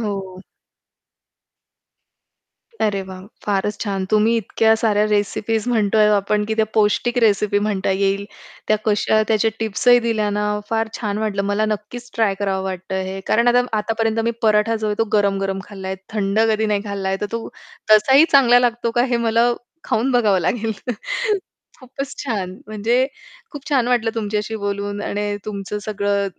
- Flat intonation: Yes, narrow, 2.0 semitones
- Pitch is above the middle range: Yes, high, 210 Hz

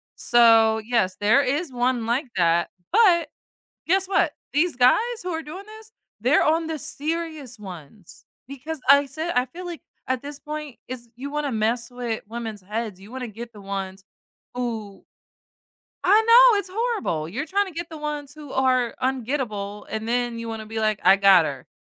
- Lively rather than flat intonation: Yes, wide, 6.0 semitones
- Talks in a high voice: Yes, very high, 250 Hz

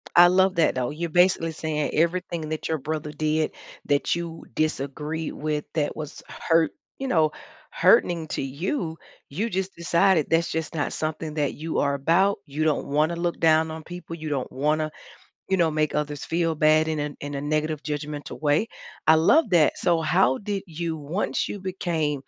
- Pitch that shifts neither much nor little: No, narrow, 2.1 semitones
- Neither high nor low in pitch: Yes, medium, 160 Hz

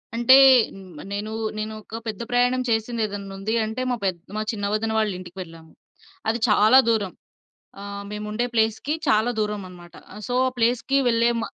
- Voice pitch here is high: Yes, high, 215 Hz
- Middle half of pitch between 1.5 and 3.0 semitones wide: Yes, narrow, 2.5 semitones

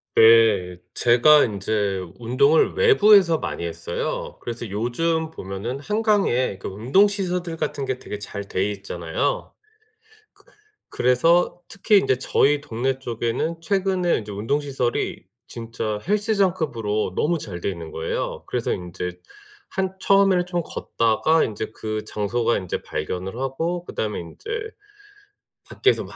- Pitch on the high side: No, low, 125 Hz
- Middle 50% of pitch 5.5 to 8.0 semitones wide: No, wide, 8.5 semitones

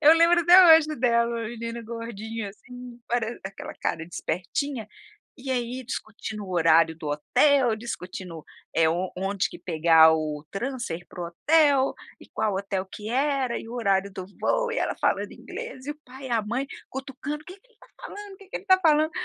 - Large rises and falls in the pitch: Yes, wide, 6.7 semitones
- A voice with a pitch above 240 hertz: No, high, 235 Hz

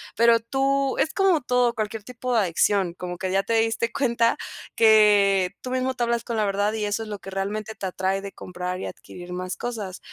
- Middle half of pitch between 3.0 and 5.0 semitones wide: Yes, average, 3.5 semitones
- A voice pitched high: Yes, high, 215 Hz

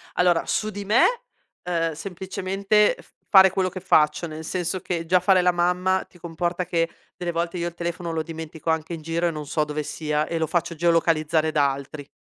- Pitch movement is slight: Yes, narrow, 2.2 semitones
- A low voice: No, medium, 170 Hz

